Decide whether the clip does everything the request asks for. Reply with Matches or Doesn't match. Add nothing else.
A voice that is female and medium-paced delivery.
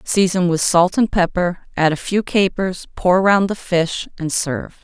Matches